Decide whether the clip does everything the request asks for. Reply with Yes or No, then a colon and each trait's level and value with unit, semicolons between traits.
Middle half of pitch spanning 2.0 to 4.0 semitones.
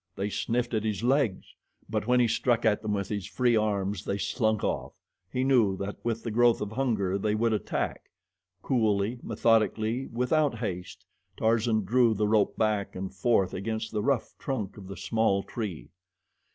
Yes: average, 2.9 semitones